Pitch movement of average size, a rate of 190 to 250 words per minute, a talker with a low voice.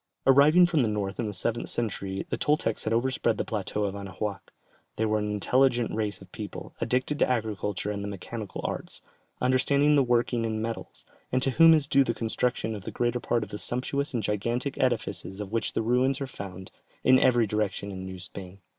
Yes: average, 3.8 semitones; fast, 205 wpm; low, 115 Hz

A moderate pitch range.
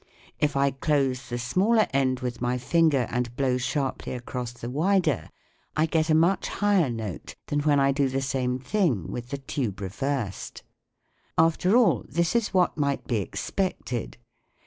Yes: average, 4.6 semitones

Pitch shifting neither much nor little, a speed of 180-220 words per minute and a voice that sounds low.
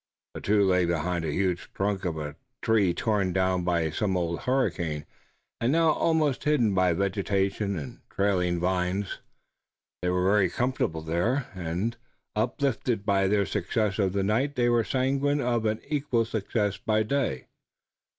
No: average, 4.7 semitones; average, 155 wpm; low, 100 Hz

